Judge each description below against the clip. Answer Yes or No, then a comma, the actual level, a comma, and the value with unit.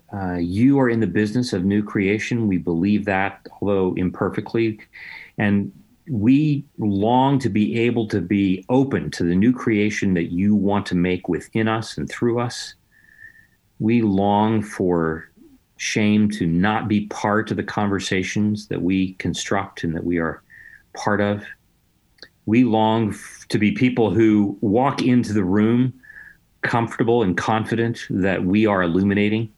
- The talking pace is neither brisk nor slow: Yes, average, 150 wpm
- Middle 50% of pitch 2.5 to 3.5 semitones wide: Yes, average, 2.9 semitones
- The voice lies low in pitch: Yes, low, 105 Hz